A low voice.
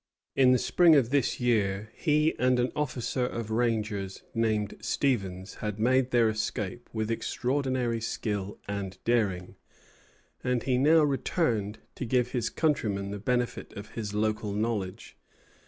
Yes: low, 115 Hz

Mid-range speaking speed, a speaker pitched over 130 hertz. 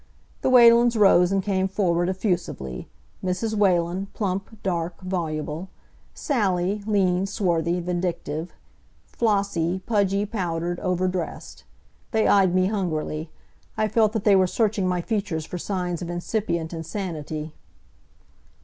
No: slow, 120 wpm; medium, 185 Hz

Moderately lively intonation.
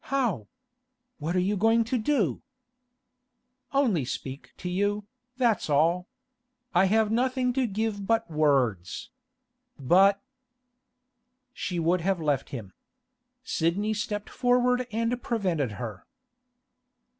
No: wide, 6.4 semitones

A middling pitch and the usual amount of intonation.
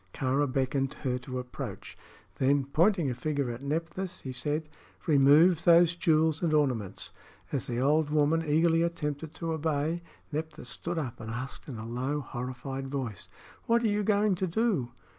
Yes: medium, 150 Hz; average, 4.0 semitones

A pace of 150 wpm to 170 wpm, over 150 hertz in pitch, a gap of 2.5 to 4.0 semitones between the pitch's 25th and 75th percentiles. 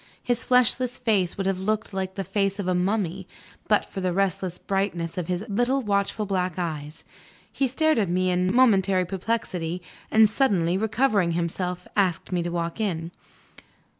Yes: average, 165 wpm; high, 190 Hz; average, 3.2 semitones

